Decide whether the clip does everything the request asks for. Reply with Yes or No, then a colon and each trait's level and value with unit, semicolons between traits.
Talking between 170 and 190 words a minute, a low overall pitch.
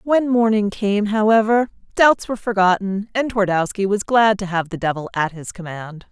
No: average, 175 wpm; high, 205 Hz